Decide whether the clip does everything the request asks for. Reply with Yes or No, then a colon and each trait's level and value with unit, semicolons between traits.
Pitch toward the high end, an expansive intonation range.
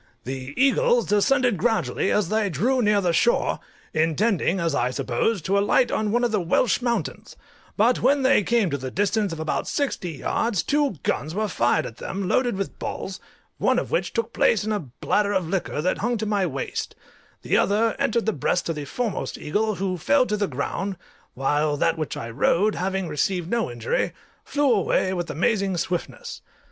Yes: high, 195 Hz; wide, 5.8 semitones